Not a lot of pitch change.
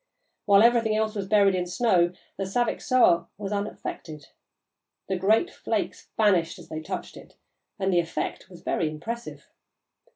No: average, 3.9 semitones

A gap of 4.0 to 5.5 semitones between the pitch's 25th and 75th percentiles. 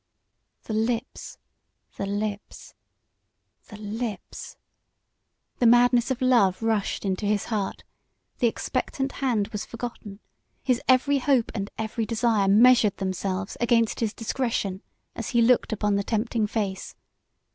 No: average, 3.0 semitones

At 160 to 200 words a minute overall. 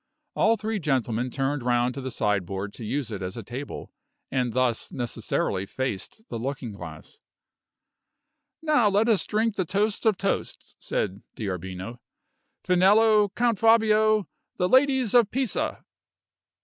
No: slow, 135 wpm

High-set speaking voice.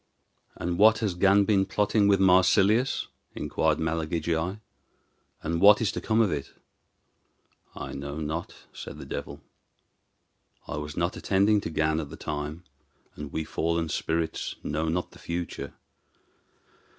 No: very low, 85 Hz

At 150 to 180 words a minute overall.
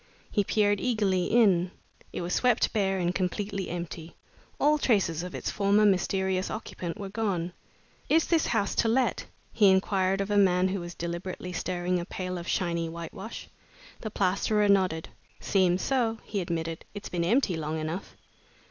Yes: average, 160 wpm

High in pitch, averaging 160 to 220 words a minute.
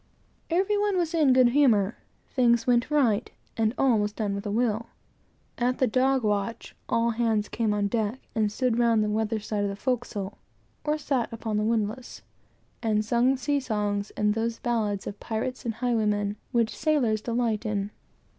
Yes: high, 230 Hz; average, 175 wpm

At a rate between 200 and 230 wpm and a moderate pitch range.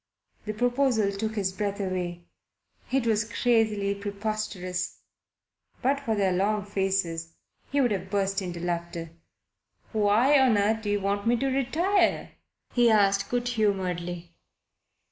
No: slow, 135 wpm; average, 3.4 semitones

